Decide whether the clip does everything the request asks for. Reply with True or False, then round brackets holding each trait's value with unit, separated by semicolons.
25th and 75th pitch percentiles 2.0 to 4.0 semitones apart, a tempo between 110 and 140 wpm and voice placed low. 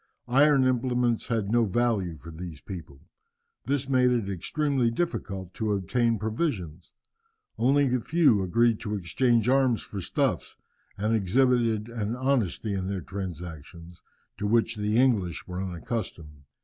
False (5.1 semitones; 135 wpm; 110 Hz)